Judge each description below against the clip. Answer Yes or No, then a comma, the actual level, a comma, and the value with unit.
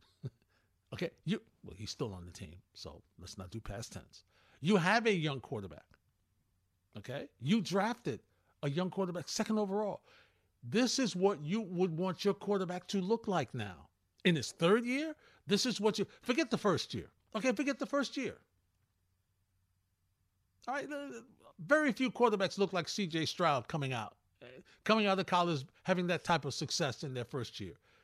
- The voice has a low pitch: No, medium, 170 Hz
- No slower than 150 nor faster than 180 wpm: Yes, average, 170 wpm